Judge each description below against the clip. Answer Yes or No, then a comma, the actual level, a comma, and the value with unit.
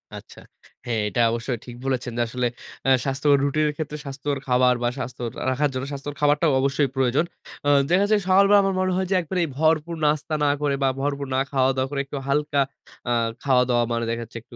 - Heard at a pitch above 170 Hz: No, medium, 140 Hz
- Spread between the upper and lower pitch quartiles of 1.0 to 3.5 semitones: Yes, average, 2.9 semitones